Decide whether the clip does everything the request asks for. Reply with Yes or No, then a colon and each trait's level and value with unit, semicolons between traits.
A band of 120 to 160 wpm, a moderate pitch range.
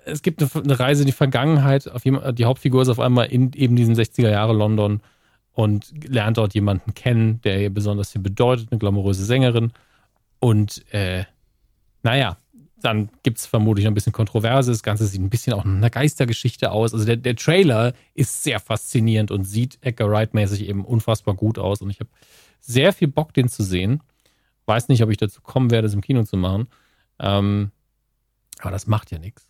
No: fast, 190 wpm; average, 3.7 semitones